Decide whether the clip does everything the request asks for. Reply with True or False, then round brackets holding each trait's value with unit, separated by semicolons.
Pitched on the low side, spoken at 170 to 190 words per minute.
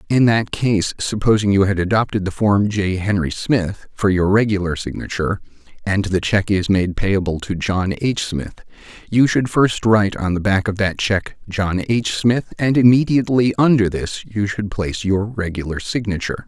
True (100 Hz; 180 wpm)